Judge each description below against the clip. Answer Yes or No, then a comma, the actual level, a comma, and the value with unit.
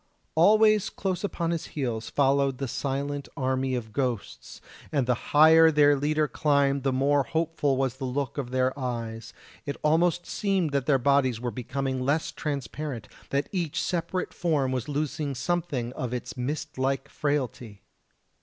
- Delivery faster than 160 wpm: No, average, 155 wpm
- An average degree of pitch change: Yes, average, 3.1 semitones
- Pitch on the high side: No, medium, 140 Hz